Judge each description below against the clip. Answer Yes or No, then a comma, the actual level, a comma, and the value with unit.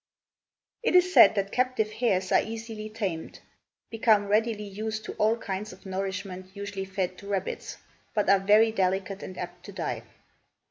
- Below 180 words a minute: Yes, average, 165 wpm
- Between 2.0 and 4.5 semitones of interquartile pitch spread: Yes, narrow, 2.4 semitones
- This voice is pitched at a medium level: No, high, 205 Hz